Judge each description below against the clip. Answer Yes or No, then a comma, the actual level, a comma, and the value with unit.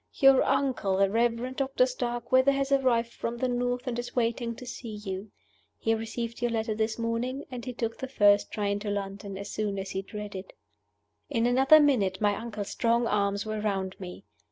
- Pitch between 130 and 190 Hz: No, high, 230 Hz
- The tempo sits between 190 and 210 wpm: Yes, average, 200 wpm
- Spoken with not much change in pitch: No, average, 3.4 semitones